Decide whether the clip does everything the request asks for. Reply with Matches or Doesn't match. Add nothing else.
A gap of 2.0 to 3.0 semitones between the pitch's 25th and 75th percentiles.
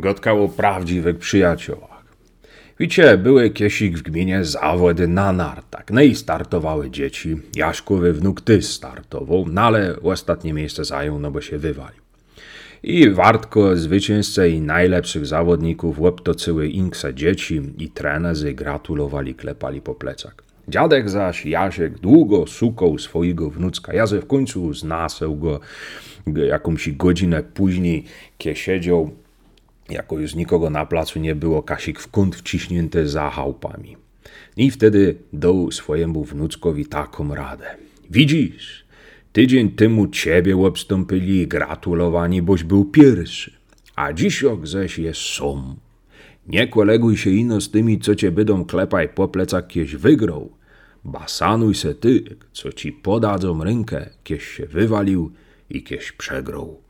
Doesn't match